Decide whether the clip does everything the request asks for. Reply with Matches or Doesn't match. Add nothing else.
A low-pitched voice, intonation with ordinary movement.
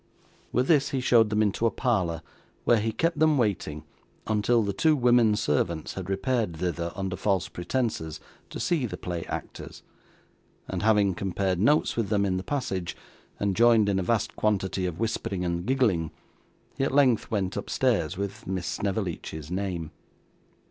Matches